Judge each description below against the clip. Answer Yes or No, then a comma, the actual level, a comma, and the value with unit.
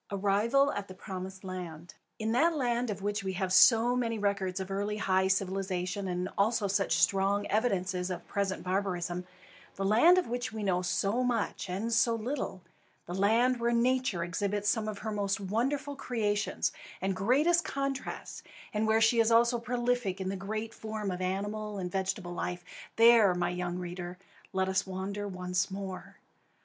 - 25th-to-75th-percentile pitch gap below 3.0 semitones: No, average, 3.4 semitones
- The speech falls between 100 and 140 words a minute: No, average, 175 wpm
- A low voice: No, high, 200 Hz